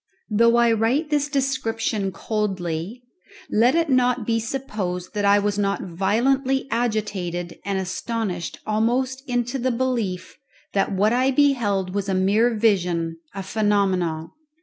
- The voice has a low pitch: No, high, 215 Hz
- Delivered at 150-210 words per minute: No, slow, 135 wpm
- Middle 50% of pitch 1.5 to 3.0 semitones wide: No, average, 4.3 semitones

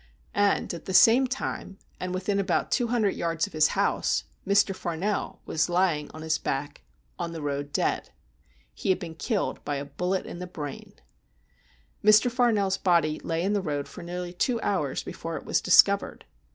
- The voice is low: No, medium, 180 Hz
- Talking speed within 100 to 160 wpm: No, average, 180 wpm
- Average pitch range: Yes, average, 4.1 semitones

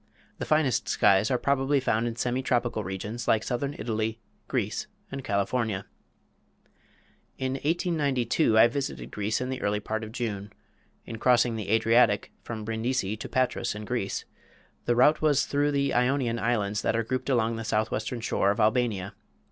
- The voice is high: No, low, 115 Hz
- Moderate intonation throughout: Yes, average, 3.2 semitones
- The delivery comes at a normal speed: Yes, average, 165 wpm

